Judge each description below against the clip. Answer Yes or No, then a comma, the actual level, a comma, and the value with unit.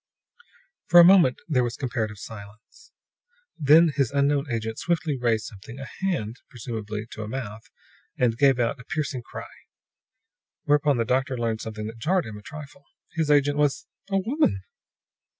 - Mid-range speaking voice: No, low, 130 Hz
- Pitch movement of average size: Yes, average, 4.8 semitones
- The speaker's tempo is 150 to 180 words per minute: Yes, average, 160 wpm